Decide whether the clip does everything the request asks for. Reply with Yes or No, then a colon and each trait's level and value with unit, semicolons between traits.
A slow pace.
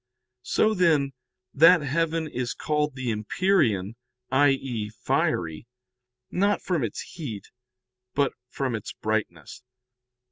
Yes: slow, 105 wpm